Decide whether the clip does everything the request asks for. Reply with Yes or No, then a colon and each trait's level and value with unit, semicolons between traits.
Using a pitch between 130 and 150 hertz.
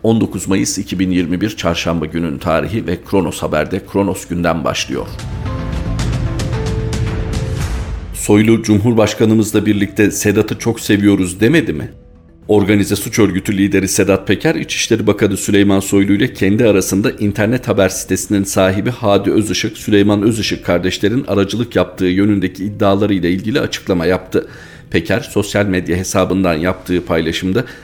No: low, 100 Hz